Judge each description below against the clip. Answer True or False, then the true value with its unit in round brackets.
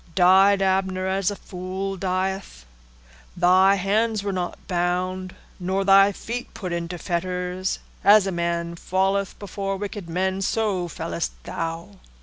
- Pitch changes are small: True (1.6 semitones)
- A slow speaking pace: True (130 wpm)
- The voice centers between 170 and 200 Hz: True (190 Hz)